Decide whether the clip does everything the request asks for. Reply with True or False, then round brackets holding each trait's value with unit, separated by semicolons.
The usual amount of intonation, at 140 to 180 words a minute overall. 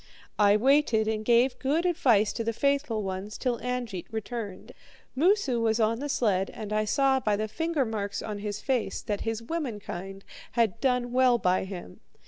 True (3.8 semitones; 170 wpm)